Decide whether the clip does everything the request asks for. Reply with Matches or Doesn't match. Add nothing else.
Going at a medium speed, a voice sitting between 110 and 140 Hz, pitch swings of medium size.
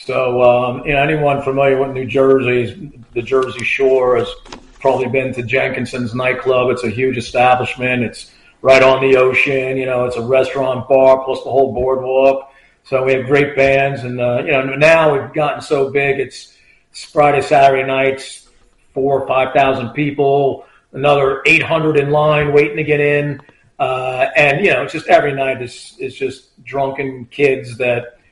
Doesn't match